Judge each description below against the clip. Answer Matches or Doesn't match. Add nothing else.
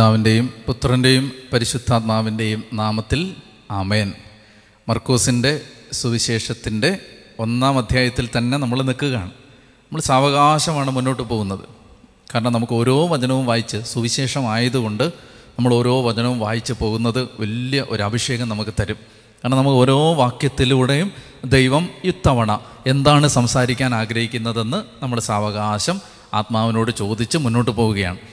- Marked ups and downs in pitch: Doesn't match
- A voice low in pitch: Matches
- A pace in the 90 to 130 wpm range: Matches